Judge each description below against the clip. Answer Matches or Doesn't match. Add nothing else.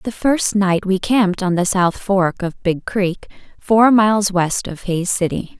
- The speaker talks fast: Doesn't match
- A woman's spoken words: Matches